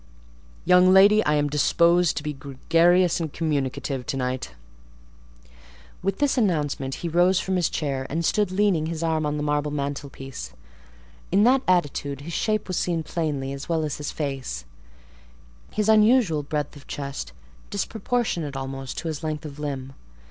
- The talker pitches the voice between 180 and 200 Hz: No, medium, 155 Hz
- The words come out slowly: No, average, 160 wpm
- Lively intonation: No, average, 4.4 semitones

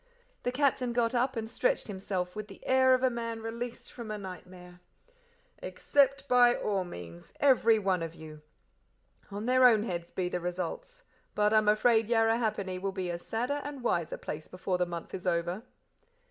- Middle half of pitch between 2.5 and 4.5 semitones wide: No, average, 5.2 semitones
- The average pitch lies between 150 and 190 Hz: No, high, 215 Hz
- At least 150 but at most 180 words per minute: Yes, average, 175 wpm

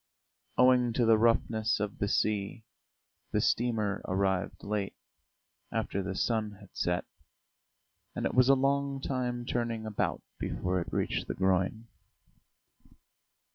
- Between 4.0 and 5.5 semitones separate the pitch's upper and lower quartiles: No, average, 3.6 semitones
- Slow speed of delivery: Yes, slow, 130 wpm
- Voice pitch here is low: Yes, low, 110 Hz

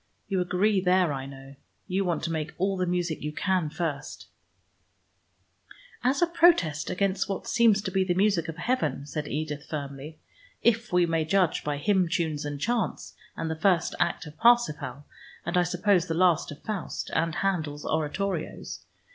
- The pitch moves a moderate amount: Yes, average, 4.2 semitones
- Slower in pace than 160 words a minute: No, average, 175 wpm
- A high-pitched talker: No, medium, 175 Hz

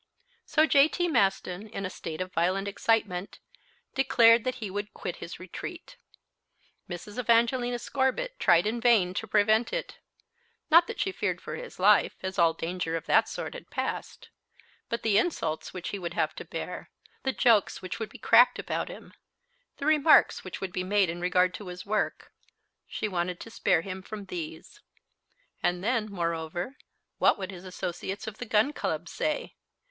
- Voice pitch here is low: No, high, 205 Hz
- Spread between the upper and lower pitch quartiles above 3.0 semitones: Yes, average, 5.1 semitones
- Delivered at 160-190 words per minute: Yes, average, 175 wpm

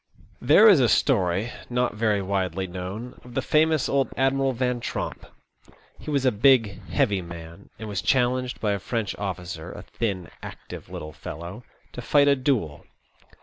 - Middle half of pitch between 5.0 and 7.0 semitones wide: Yes, wide, 5.6 semitones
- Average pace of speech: Yes, average, 165 wpm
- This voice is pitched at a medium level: No, low, 115 Hz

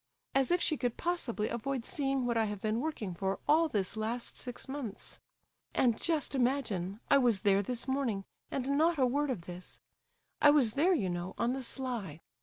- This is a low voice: No, high, 245 Hz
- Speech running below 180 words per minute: No, average, 195 wpm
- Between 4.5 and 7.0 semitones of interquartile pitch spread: Yes, average, 4.9 semitones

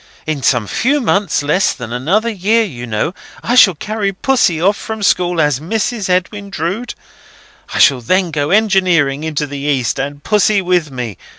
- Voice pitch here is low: No, medium, 175 Hz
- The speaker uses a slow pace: No, average, 175 wpm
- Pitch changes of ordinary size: No, wide, 6.3 semitones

